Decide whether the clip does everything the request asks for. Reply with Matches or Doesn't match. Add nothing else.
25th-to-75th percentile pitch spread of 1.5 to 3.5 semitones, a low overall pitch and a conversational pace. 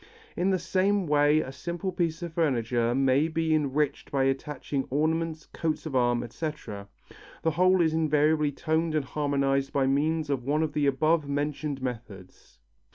Doesn't match